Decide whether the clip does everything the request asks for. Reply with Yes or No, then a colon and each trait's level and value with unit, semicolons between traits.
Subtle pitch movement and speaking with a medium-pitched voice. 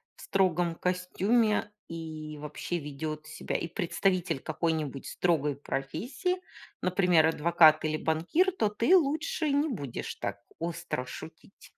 No: average, 5.0 semitones; medium, 170 Hz